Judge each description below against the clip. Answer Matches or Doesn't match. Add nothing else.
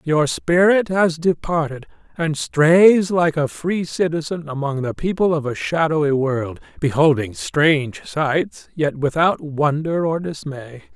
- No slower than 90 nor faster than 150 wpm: Matches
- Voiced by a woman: Doesn't match